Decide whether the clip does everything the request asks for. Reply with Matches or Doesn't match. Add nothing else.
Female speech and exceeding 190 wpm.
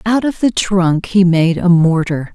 Matches